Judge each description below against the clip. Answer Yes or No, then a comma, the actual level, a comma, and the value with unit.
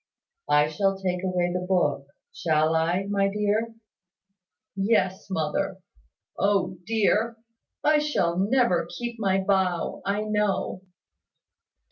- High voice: Yes, high, 195 Hz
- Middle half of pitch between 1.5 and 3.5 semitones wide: Yes, average, 2.9 semitones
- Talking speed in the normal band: No, slow, 110 wpm